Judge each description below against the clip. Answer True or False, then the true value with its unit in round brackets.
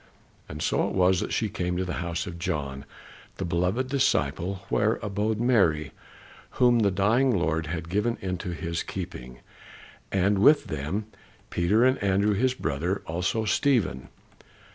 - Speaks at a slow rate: False (150 wpm)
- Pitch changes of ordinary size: True (4.4 semitones)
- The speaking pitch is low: True (95 Hz)